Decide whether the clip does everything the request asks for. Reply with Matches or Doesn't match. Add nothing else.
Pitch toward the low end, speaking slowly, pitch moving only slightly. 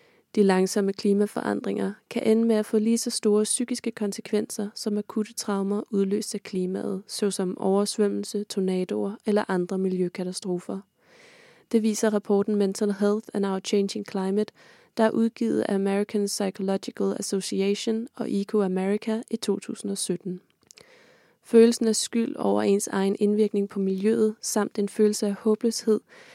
Doesn't match